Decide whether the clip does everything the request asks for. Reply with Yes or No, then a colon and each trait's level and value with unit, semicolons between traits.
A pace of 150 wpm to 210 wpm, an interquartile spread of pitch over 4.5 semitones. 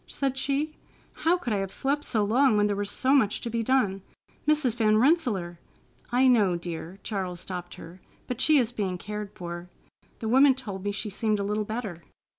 Yes: average, 200 wpm; average, 5.1 semitones